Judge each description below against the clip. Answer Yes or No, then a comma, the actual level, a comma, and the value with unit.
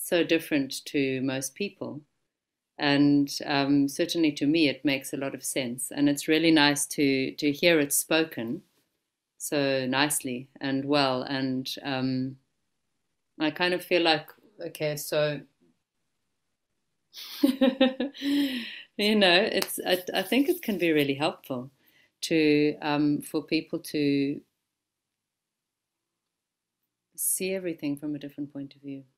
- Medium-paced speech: No, slow, 130 wpm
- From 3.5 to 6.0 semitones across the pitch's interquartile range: Yes, average, 3.8 semitones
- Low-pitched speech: No, medium, 150 Hz